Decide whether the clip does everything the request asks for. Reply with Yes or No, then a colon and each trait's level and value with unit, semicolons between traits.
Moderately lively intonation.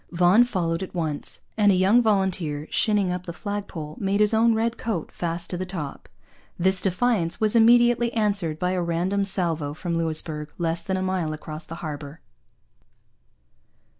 Yes: average, 3.8 semitones